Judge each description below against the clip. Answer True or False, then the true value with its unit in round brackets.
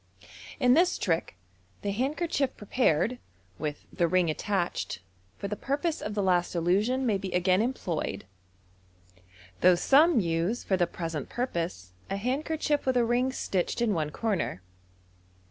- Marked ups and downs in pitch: True (6.5 semitones)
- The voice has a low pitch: False (205 Hz)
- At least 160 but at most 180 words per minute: False (145 wpm)